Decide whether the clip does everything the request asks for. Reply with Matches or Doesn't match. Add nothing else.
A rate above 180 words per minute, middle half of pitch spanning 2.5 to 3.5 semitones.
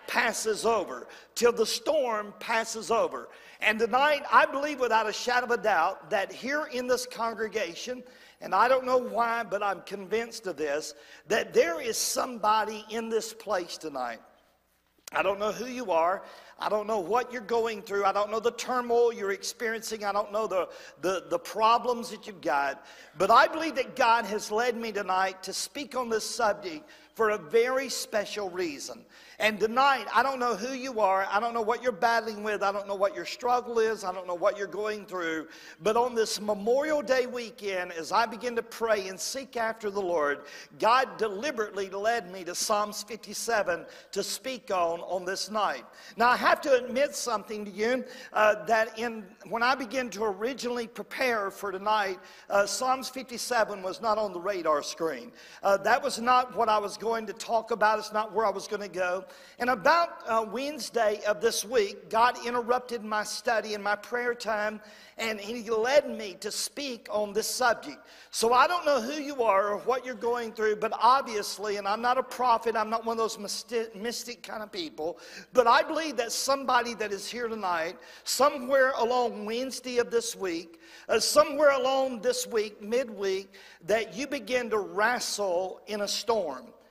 Matches